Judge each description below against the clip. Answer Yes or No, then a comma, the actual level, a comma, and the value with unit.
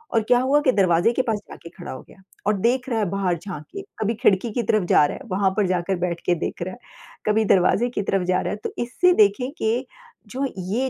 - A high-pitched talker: Yes, high, 210 Hz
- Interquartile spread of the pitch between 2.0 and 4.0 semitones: No, average, 4.8 semitones